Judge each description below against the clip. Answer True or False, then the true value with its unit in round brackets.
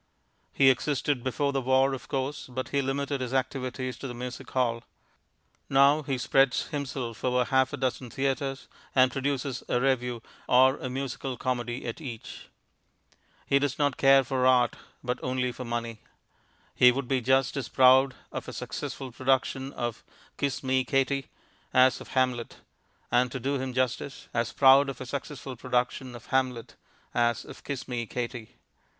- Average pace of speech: True (165 wpm)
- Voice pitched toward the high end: False (130 Hz)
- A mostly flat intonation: True (1.5 semitones)